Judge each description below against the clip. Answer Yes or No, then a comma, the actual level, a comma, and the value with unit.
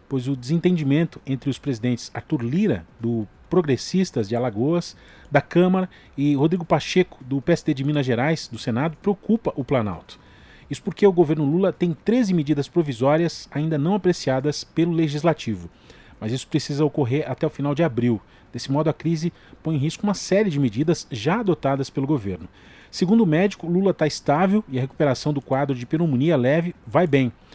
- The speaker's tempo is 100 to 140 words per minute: No, average, 175 wpm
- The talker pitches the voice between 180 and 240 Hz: No, medium, 150 Hz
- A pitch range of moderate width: Yes, average, 4.4 semitones